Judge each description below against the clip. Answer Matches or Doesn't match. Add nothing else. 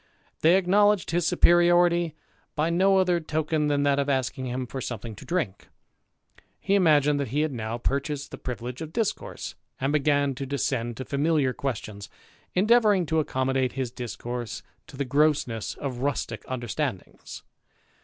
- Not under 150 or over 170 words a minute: Matches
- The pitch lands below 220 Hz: Matches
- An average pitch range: Matches